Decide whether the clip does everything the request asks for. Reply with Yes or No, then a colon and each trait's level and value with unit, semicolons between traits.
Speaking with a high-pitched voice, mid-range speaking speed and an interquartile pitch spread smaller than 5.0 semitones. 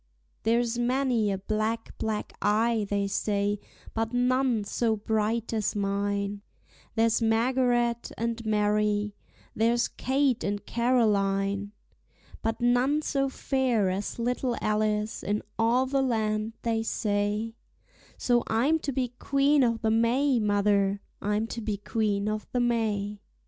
No: high, 225 Hz; slow, 130 wpm; narrow, 2.6 semitones